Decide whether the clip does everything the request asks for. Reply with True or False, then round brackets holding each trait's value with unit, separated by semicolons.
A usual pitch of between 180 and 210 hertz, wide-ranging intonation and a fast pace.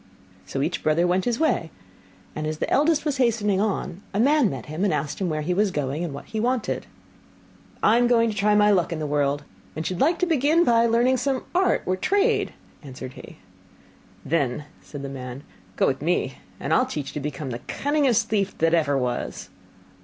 True (190 Hz; 8.5 semitones; 215 wpm)